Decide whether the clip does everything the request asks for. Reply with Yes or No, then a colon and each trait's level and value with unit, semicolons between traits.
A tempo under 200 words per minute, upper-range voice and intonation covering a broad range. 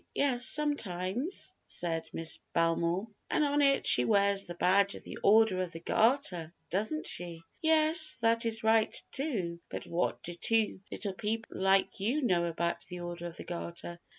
Yes: average, 170 wpm; high, 200 Hz; wide, 5.7 semitones